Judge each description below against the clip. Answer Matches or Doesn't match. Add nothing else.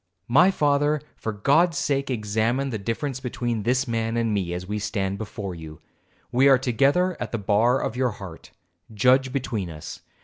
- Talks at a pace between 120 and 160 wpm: Doesn't match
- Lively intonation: Doesn't match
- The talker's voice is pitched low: Matches